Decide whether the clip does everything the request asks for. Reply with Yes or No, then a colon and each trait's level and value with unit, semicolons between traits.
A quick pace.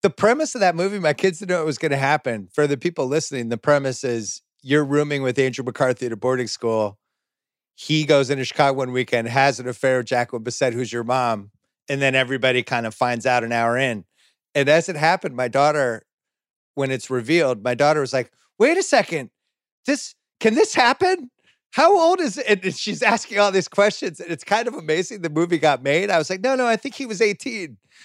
Yes: fast, 220 wpm